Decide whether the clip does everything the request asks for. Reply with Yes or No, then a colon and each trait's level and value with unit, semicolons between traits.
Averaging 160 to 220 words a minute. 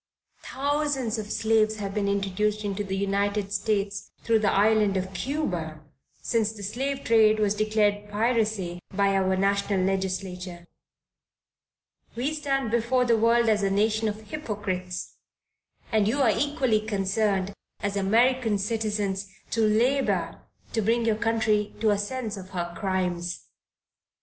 No: average, 140 wpm